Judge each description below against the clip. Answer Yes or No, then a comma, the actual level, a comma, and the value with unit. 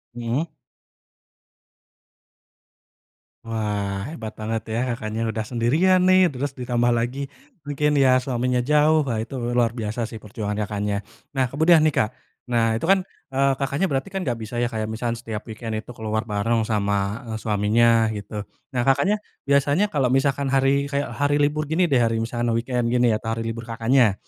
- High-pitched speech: No, low, 120 Hz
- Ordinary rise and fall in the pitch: Yes, average, 3.9 semitones